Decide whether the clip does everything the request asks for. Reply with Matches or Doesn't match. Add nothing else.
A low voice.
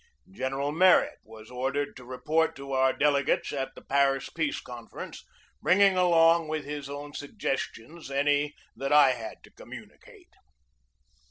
Doesn't match